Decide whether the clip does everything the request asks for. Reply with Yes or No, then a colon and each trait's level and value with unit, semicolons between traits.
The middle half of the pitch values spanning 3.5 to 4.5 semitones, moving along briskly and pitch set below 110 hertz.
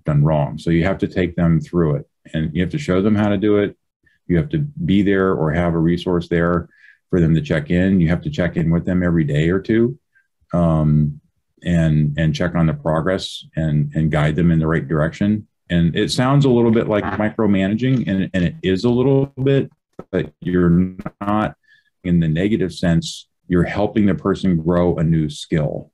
Yes: average, 4.1 semitones; fast, 210 wpm; very low, 90 Hz